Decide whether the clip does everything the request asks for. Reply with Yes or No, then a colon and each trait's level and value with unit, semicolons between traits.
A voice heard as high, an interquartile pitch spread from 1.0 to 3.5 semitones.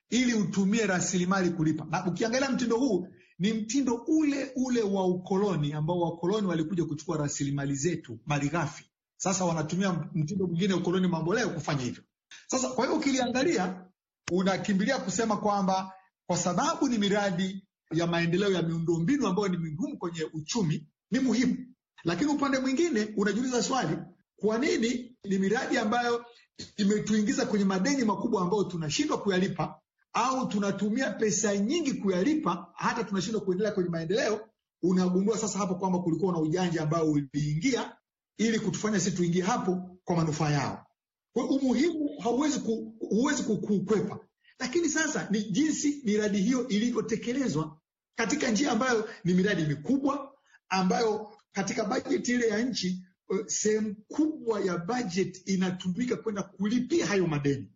No: high, 200 Hz; average, 4.8 semitones